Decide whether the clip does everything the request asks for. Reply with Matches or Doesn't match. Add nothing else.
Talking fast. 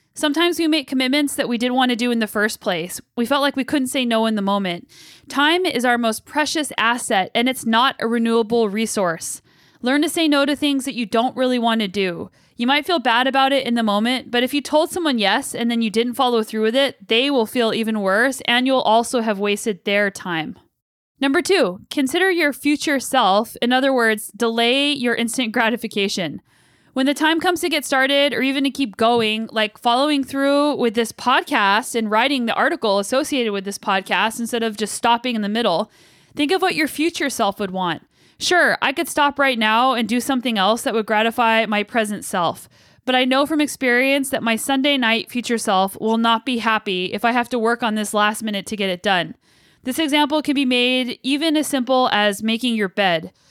Matches